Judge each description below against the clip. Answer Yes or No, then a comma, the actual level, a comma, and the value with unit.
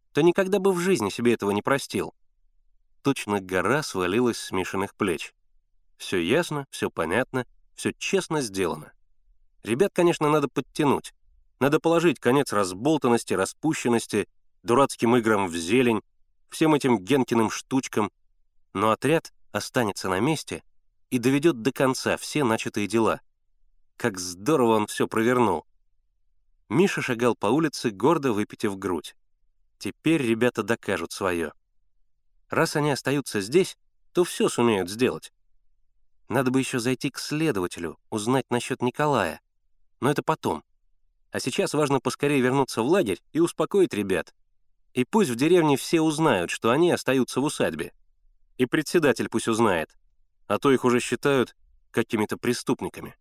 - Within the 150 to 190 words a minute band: No, average, 135 wpm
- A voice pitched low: Yes, low, 120 Hz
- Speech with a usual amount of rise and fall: No, wide, 5.8 semitones